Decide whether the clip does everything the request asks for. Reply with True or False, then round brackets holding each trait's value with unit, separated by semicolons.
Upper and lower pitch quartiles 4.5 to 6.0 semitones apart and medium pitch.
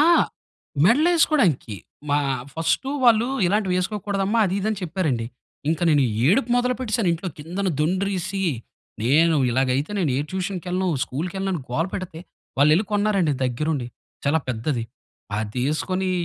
True (4.9 semitones; 180 Hz)